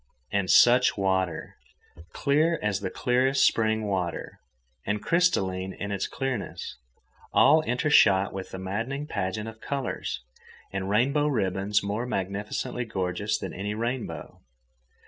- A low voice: Yes, low, 105 Hz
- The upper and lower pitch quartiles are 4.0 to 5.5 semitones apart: Yes, average, 4.7 semitones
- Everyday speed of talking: No, slow, 120 wpm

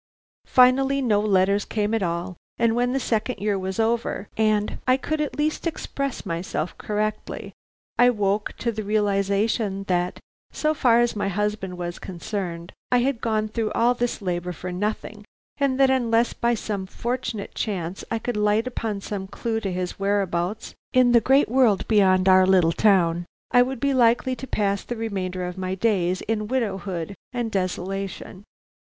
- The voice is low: No, high, 210 Hz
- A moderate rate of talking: Yes, average, 170 wpm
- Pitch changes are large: No, average, 3.9 semitones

